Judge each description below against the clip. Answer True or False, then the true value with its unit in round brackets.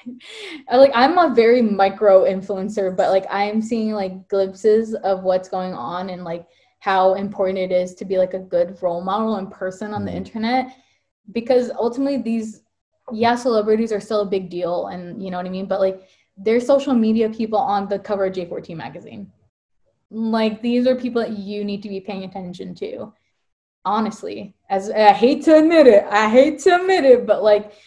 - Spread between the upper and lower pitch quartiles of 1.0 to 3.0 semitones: False (3.6 semitones)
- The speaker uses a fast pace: False (190 wpm)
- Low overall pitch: False (210 Hz)